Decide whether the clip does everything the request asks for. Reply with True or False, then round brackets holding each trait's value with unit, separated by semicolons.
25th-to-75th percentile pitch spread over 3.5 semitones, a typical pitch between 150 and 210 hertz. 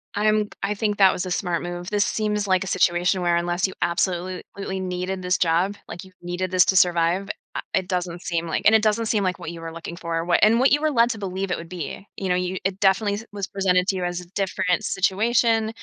False (2.5 semitones; 185 Hz)